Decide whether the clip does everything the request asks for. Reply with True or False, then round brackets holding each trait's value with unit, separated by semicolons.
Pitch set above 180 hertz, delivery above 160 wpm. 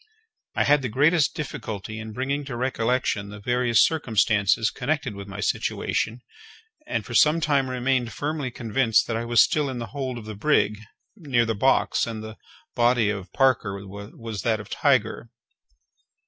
False (120 Hz; 170 wpm)